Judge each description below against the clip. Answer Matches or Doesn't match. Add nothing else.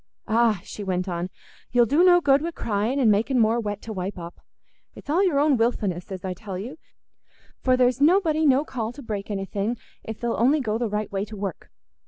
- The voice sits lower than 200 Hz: Doesn't match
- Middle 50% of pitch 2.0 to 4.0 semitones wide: Doesn't match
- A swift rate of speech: Matches